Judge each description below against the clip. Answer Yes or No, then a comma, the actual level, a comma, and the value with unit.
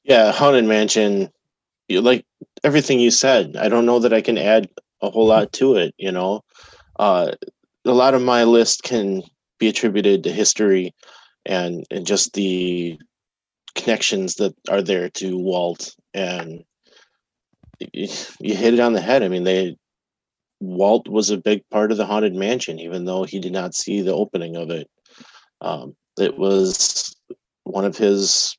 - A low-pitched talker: Yes, low, 100 Hz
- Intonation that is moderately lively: Yes, average, 3.3 semitones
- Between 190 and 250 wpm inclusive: No, average, 160 wpm